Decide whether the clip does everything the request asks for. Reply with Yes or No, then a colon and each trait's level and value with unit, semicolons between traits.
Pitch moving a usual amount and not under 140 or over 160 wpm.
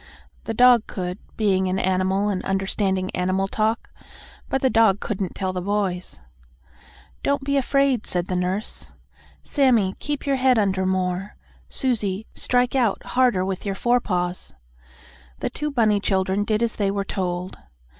Yes: average, 4.2 semitones; average, 150 wpm